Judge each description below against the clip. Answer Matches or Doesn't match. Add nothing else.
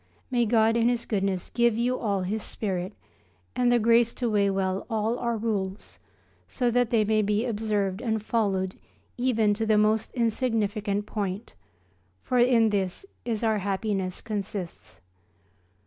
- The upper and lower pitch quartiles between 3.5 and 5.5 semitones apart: Doesn't match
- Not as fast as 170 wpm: Matches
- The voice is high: Matches